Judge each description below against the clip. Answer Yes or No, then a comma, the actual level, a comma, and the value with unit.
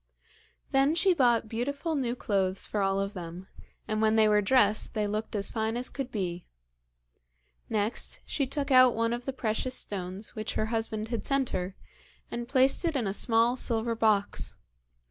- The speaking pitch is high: Yes, high, 225 Hz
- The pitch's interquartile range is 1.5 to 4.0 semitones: Yes, average, 3.5 semitones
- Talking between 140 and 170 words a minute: No, average, 180 wpm